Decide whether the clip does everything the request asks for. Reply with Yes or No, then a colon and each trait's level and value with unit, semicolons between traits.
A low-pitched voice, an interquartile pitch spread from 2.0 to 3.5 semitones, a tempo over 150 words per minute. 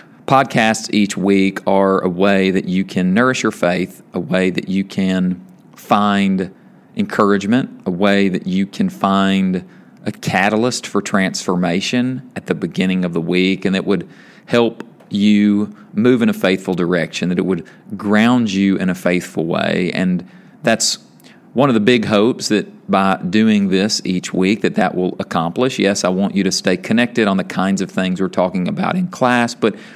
Yes: very low, 95 Hz; average, 3.0 semitones; average, 180 wpm